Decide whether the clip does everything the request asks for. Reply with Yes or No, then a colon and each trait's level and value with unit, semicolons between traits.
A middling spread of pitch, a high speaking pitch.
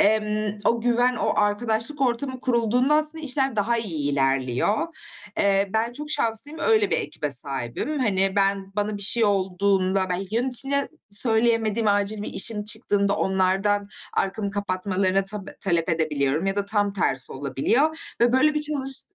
Yes: average, 3.9 semitones; high, 210 Hz